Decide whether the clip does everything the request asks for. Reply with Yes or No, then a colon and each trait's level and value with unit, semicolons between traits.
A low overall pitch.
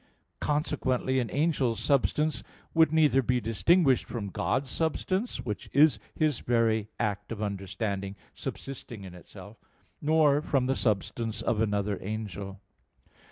Yes: low, 120 Hz